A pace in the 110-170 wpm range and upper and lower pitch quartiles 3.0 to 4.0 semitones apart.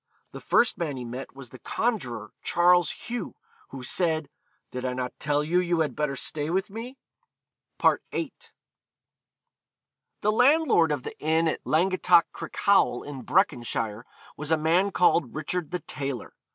No: average, 150 wpm; average, 5.2 semitones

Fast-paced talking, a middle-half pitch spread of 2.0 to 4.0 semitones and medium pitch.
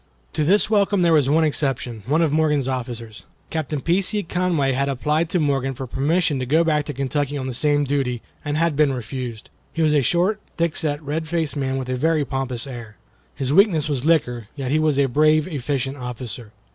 Yes: fast, 210 wpm; average, 3.4 semitones; medium, 145 Hz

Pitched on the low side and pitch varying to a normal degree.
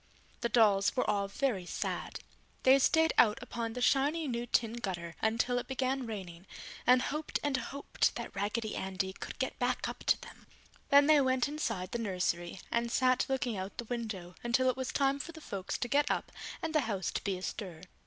No: high, 235 Hz; average, 5.0 semitones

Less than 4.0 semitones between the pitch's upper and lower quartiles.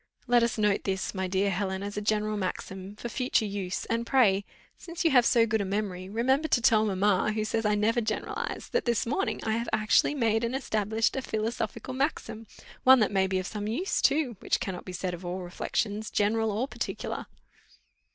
Yes: average, 3.0 semitones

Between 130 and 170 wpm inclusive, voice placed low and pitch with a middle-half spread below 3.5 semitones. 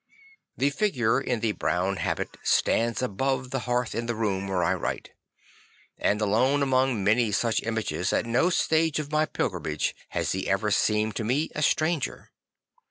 No: average, 165 wpm; low, 120 Hz; average, 4.2 semitones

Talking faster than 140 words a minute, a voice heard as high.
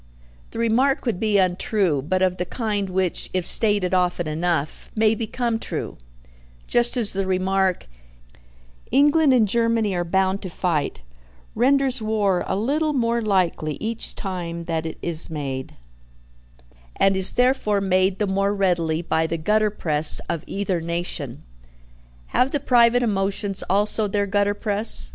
Yes: average, 150 wpm; high, 195 Hz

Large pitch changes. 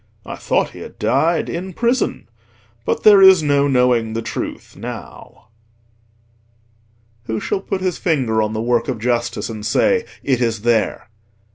Yes: wide, 8.2 semitones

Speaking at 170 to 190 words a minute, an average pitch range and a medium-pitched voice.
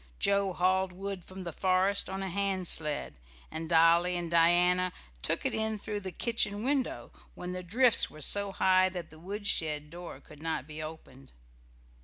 Yes: average, 175 wpm; average, 3.2 semitones; medium, 180 Hz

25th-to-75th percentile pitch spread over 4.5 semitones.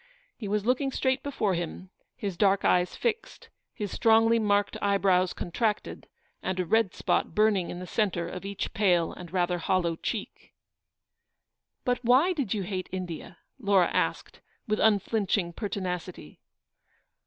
No: average, 3.6 semitones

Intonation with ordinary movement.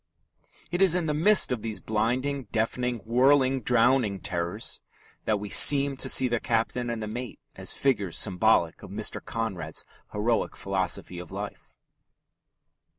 Yes: average, 4.1 semitones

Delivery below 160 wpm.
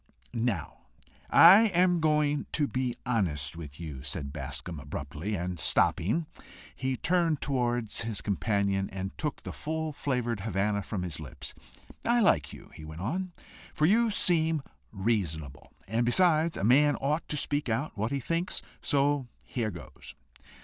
Yes: average, 150 wpm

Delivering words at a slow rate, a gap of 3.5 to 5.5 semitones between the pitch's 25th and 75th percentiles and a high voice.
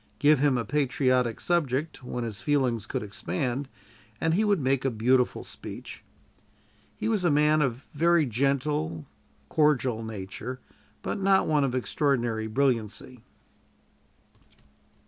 No: slow, 125 wpm; average, 4.1 semitones; low, 130 Hz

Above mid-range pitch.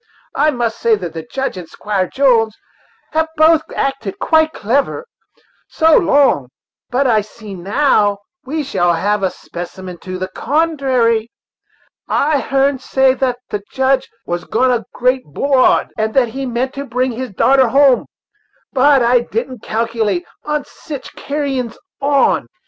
Yes: very high, 250 Hz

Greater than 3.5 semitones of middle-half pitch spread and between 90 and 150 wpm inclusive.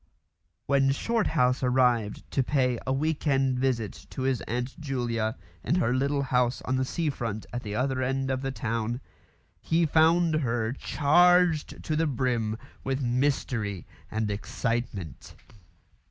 No: average, 3.1 semitones; average, 145 wpm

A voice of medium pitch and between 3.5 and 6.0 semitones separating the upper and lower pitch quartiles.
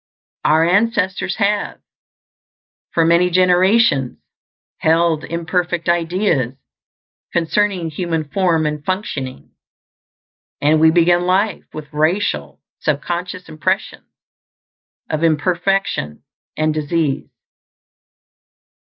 No: medium, 170 Hz; average, 3.1 semitones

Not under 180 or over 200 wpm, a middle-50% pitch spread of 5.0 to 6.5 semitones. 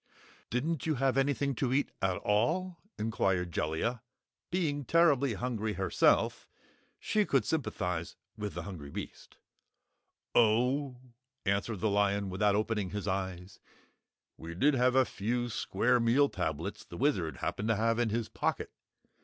No: average, 140 wpm; average, 5.3 semitones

